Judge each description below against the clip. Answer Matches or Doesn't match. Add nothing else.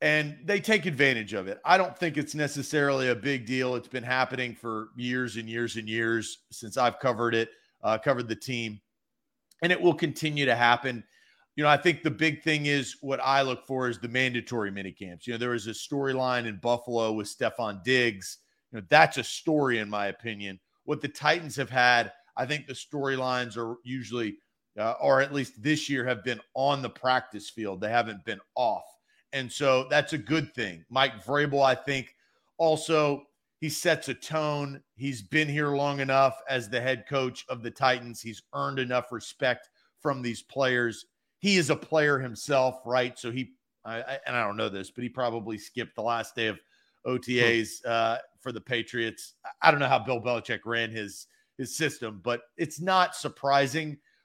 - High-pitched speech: Doesn't match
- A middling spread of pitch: Matches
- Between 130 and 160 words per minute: Doesn't match